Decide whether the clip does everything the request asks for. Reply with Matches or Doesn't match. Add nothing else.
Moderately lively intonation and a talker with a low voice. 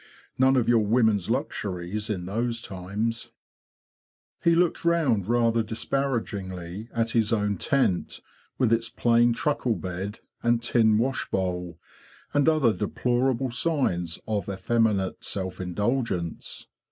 Matches